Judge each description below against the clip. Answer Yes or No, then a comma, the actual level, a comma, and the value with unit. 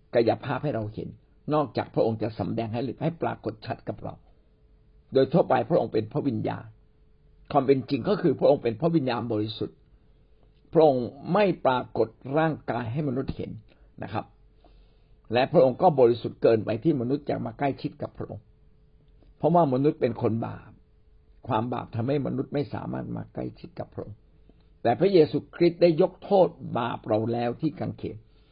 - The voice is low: Yes, low, 125 Hz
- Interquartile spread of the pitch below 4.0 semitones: No, average, 5.3 semitones